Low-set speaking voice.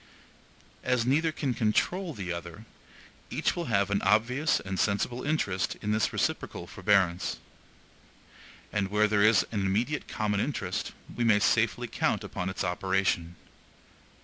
Yes: low, 105 Hz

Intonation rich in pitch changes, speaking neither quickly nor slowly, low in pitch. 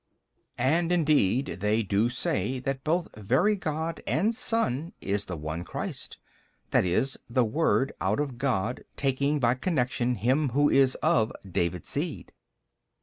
Yes: wide, 5.8 semitones; average, 145 wpm; low, 130 Hz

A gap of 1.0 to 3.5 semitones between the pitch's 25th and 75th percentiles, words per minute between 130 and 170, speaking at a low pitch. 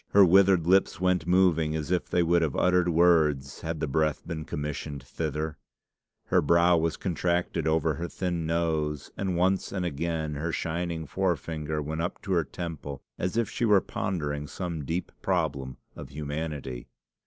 Yes: average, 2.8 semitones; average, 165 wpm; very low, 80 Hz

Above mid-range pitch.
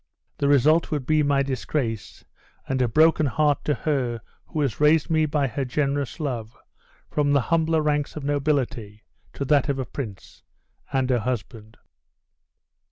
No: medium, 140 Hz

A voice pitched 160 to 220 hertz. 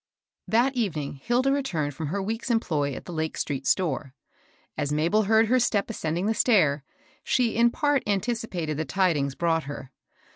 Yes: medium, 185 Hz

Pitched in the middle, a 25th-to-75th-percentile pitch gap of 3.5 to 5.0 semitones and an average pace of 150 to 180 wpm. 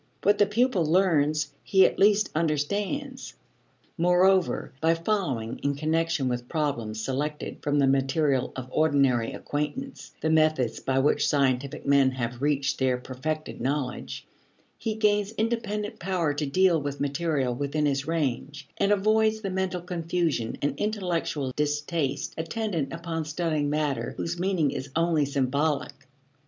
No: medium, 155 Hz; average, 4.6 semitones; average, 140 wpm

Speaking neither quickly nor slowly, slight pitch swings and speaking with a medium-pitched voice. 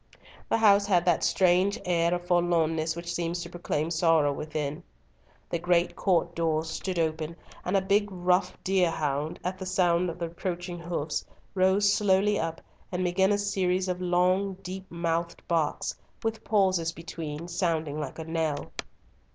Yes: average, 160 wpm; narrow, 2.3 semitones; medium, 175 Hz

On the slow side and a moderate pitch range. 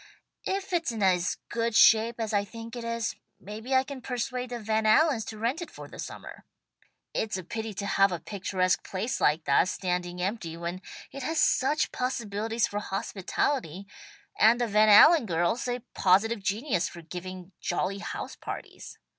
No: average, 175 wpm; average, 4.4 semitones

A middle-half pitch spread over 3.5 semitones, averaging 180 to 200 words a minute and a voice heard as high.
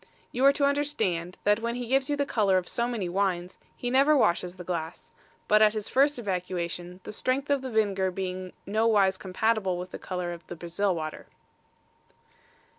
Yes: average, 5.2 semitones; average, 190 wpm; high, 200 Hz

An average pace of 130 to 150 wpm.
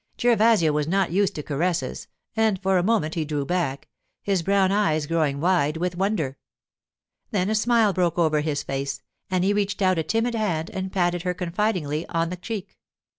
No: average, 185 wpm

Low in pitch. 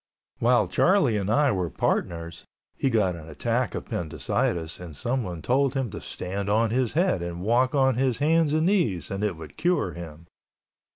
Yes: low, 110 Hz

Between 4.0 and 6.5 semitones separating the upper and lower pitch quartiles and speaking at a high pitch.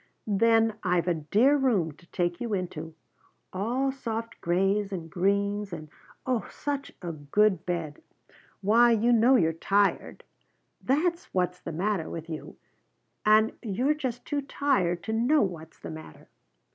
Yes: average, 5.3 semitones; high, 205 Hz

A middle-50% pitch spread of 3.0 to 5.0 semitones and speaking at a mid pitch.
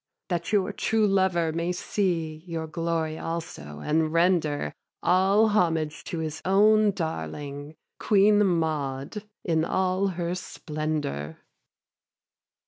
Yes: average, 3.4 semitones; medium, 170 Hz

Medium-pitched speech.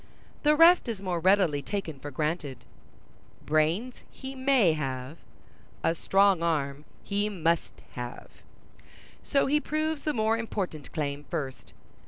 Yes: medium, 175 Hz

